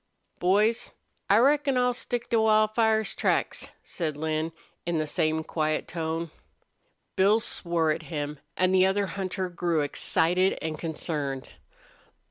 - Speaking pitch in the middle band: Yes, medium, 175 Hz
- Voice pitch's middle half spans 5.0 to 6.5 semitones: Yes, average, 5.3 semitones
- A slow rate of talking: Yes, slow, 130 wpm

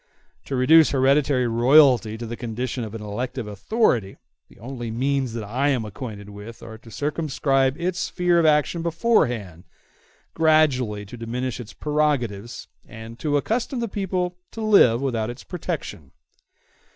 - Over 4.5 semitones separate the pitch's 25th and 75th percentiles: Yes, average, 5.2 semitones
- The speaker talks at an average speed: Yes, average, 150 wpm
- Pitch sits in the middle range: No, low, 130 Hz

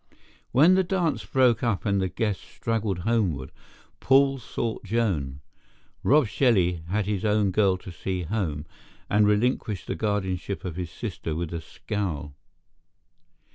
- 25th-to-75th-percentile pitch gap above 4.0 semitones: Yes, average, 4.4 semitones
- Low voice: Yes, low, 105 Hz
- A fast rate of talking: No, average, 140 wpm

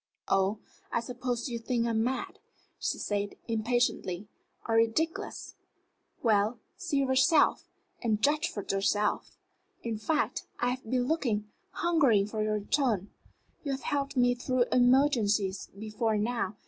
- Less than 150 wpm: Yes, slow, 135 wpm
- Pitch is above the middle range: Yes, high, 235 Hz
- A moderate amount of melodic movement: Yes, average, 3.6 semitones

